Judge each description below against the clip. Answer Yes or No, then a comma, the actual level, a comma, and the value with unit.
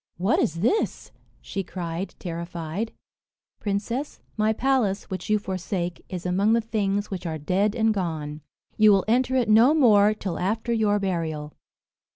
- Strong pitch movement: No, average, 3.9 semitones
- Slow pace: No, average, 155 wpm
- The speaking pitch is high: Yes, high, 200 Hz